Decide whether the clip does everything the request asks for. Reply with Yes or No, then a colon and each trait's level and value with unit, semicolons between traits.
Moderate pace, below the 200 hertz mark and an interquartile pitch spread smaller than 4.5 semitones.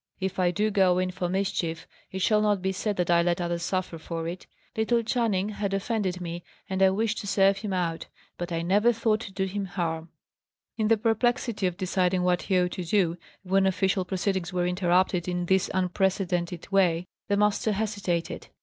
Yes: average, 195 wpm; high, 190 Hz; narrow, 2.4 semitones